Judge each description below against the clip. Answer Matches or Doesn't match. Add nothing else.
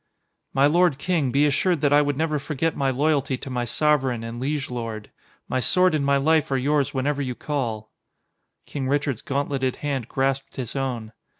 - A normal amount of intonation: Doesn't match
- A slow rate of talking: Doesn't match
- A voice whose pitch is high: Doesn't match